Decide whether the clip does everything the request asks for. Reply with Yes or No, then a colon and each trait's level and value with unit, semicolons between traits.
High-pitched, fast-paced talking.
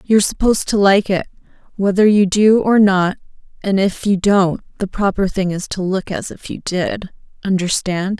No: high, 195 Hz; average, 185 wpm